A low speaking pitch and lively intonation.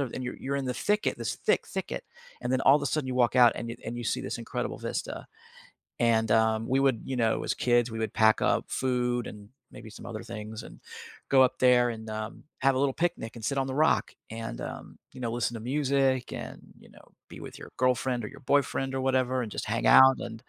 No: low, 125 Hz; average, 2.7 semitones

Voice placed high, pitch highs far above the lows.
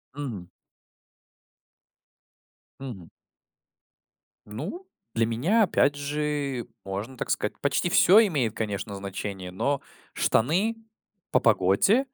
No: low, 130 Hz; wide, 6.7 semitones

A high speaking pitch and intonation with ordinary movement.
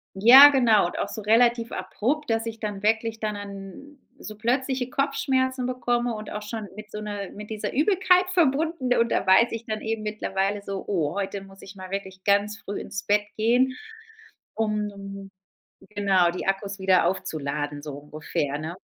Yes: high, 210 Hz; average, 3.6 semitones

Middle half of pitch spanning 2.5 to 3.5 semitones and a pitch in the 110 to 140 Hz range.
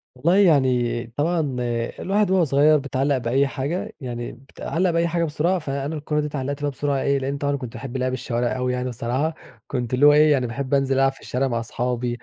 Yes: average, 3.0 semitones; low, 135 Hz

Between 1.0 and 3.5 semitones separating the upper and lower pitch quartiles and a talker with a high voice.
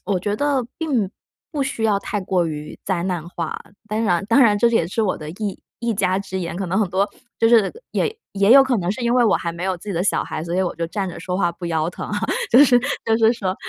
No: average, 4.3 semitones; high, 195 Hz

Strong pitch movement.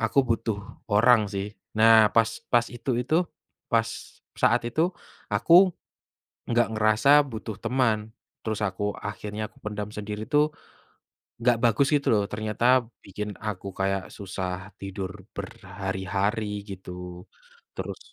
No: average, 2.9 semitones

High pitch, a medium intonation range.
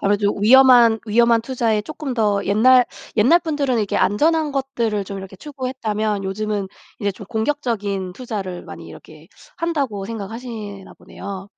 Yes: high, 220 Hz; average, 4.1 semitones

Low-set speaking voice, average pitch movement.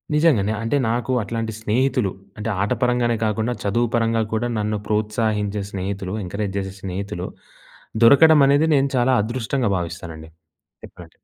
Yes: low, 110 Hz; average, 3.4 semitones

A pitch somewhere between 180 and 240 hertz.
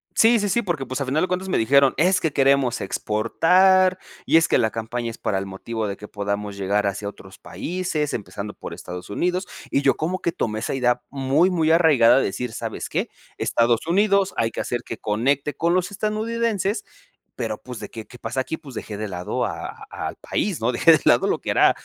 No: low, 135 Hz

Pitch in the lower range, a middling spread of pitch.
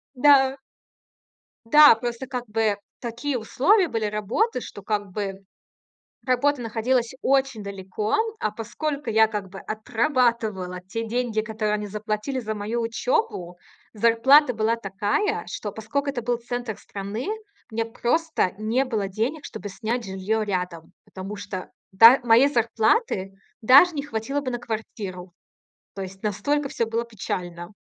No: high, 225 Hz; average, 3.6 semitones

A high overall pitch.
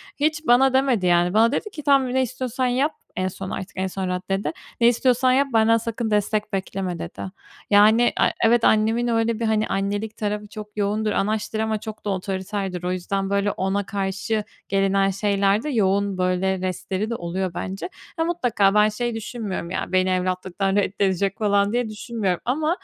Yes: high, 205 Hz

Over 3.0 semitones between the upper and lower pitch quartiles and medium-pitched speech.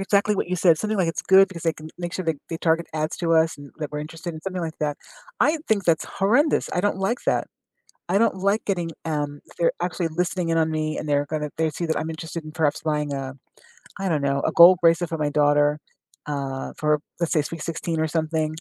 No: average, 2.7 semitones; medium, 165 Hz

